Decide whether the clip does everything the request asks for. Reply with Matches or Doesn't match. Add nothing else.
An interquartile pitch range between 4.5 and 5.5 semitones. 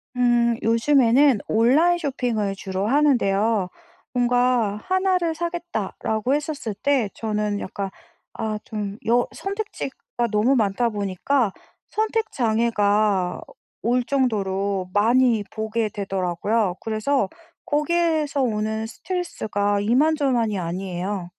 Matches